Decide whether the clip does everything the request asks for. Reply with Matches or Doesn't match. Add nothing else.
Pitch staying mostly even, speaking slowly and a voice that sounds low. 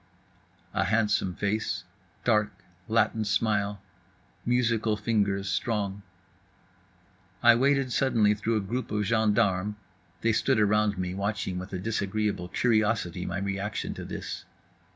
Matches